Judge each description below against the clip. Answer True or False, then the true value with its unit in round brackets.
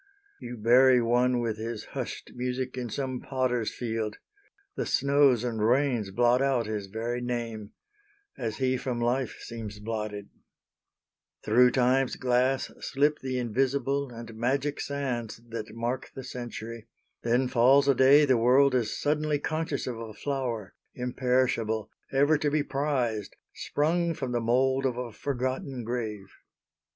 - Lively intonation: False (2.6 semitones)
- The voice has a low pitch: True (125 Hz)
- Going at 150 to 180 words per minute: False (140 wpm)